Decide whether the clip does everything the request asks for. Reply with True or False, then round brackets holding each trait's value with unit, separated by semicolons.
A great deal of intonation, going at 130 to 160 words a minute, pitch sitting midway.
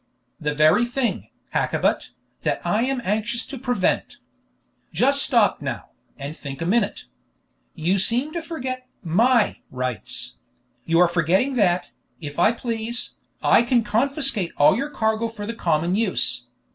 False (6.6 semitones; 145 wpm; 220 Hz)